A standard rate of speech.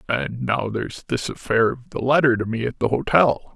No: fast, 220 wpm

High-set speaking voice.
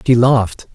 No: low, 115 Hz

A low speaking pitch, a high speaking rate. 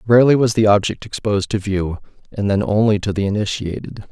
No: low, 105 Hz; average, 190 wpm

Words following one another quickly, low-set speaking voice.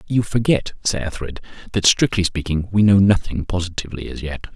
No: average, 160 wpm; very low, 95 Hz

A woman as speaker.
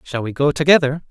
No: male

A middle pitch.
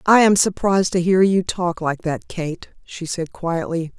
Yes: medium, 175 Hz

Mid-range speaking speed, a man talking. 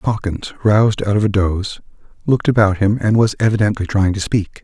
Yes: average, 195 wpm; male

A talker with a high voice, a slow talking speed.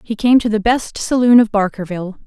No: high, 220 Hz; fast, 210 wpm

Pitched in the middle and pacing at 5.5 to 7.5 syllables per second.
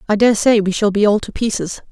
No: high, 210 Hz; 6.0 syllables/s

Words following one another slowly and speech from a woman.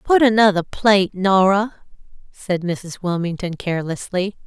Yes: slow, 110 wpm; female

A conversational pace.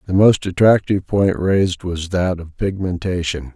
Yes: average, 150 wpm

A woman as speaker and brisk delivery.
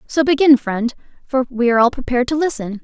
Yes: female; fast, 210 wpm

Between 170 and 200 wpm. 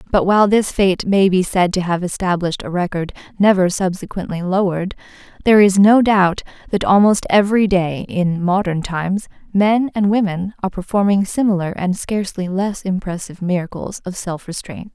No: average, 160 wpm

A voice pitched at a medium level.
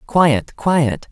Yes: medium, 150 Hz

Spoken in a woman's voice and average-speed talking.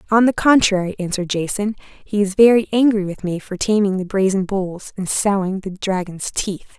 Yes: female; average, 185 wpm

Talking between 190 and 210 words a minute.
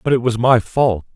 No: fast, 260 wpm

